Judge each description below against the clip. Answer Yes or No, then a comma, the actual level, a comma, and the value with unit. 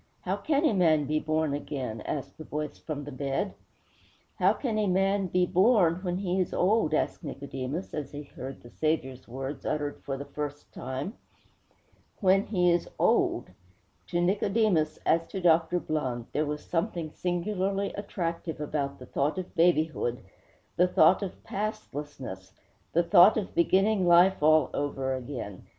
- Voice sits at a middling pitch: Yes, medium, 165 Hz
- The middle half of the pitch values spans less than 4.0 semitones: No, average, 4.5 semitones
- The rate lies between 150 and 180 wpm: Yes, average, 160 wpm